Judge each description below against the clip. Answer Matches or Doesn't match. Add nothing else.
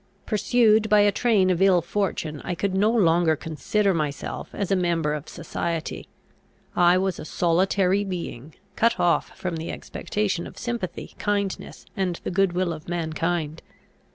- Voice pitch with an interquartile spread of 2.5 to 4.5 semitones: Matches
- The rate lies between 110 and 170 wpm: Matches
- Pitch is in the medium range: Matches